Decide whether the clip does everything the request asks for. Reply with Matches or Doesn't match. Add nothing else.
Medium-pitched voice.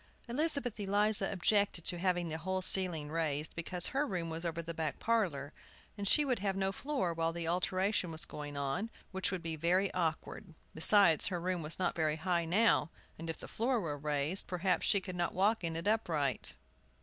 Matches